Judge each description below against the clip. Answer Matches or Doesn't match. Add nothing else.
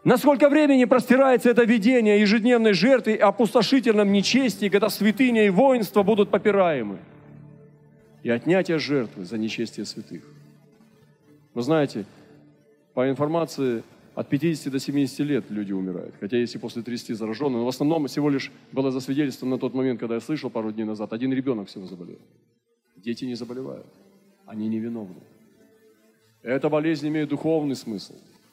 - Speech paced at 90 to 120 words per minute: Doesn't match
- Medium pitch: Matches